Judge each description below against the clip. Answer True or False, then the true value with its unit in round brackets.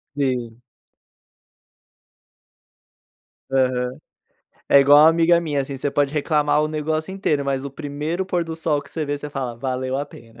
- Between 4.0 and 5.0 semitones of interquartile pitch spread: False (2.8 semitones)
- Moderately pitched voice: True (145 Hz)